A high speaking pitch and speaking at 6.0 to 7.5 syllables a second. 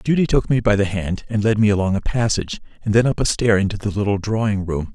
No: low, 105 Hz; 6.2 syllables/s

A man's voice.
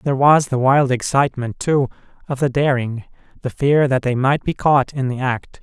Yes: male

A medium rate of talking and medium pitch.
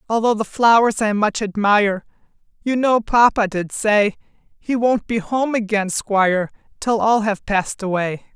No: average, 160 wpm; high, 215 Hz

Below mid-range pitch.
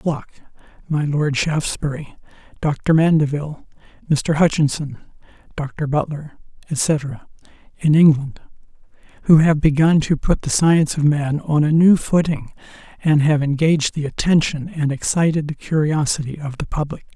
No: medium, 150 Hz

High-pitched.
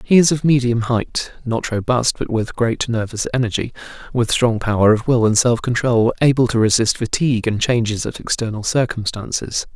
No: low, 120 Hz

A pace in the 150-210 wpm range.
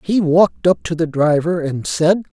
Yes: average, 200 wpm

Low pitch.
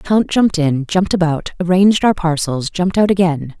No: medium, 175 Hz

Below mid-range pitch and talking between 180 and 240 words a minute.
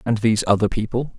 Yes: low, 110 Hz; fast, 205 wpm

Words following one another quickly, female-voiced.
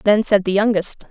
Yes: fast, 215 wpm; female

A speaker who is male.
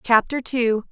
No: female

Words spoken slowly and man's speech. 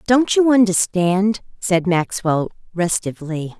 No: slow, 100 wpm; female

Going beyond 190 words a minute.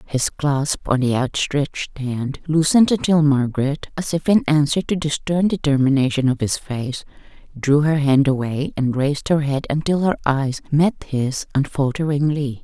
No: average, 160 wpm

